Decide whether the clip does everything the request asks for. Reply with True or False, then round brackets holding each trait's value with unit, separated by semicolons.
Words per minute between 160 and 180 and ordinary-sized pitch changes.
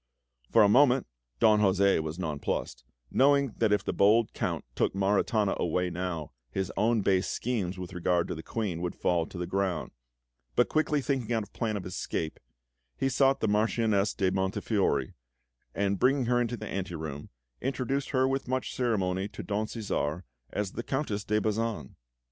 True (175 wpm; 4.4 semitones)